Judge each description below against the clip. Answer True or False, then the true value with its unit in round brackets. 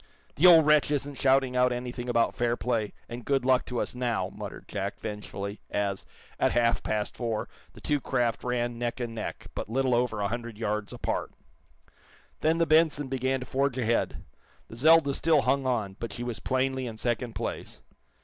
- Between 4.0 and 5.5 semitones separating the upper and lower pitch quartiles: False (2.8 semitones)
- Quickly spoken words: False (190 wpm)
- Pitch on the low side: True (125 Hz)